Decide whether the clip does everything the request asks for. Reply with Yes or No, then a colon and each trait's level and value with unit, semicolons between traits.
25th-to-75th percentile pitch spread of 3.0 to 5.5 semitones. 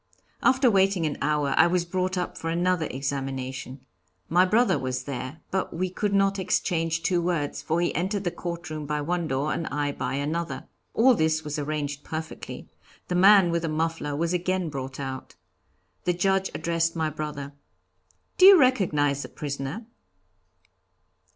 Yes: average, 3.9 semitones